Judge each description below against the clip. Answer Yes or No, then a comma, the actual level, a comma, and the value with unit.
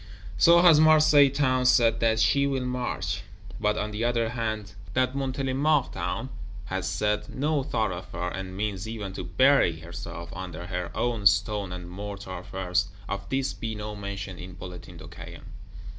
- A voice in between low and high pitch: No, low, 105 Hz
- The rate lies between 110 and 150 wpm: No, average, 160 wpm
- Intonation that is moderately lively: No, wide, 5.7 semitones